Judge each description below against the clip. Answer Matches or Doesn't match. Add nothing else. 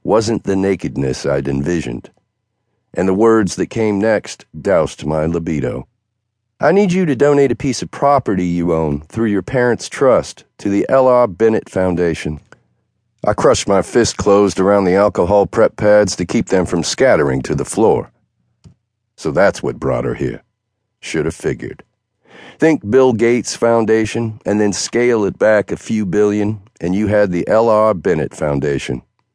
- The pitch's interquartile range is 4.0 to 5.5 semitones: Matches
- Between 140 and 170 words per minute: Matches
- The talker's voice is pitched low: Matches